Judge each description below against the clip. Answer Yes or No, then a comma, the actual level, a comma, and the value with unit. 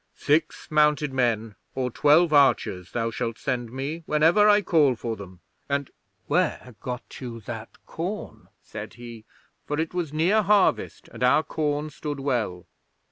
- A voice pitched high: No, medium, 140 Hz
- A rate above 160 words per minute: No, average, 150 wpm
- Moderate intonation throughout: Yes, average, 4.5 semitones